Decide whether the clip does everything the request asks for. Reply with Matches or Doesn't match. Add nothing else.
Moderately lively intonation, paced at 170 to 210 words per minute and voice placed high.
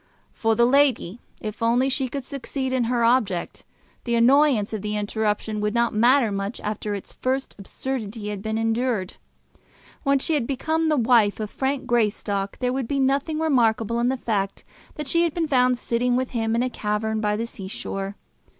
Matches